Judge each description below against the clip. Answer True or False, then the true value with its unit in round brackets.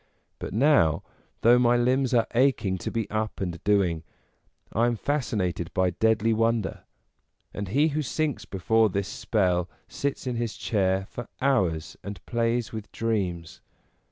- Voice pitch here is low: True (110 Hz)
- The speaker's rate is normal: True (155 wpm)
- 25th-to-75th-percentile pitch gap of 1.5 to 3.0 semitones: False (4.2 semitones)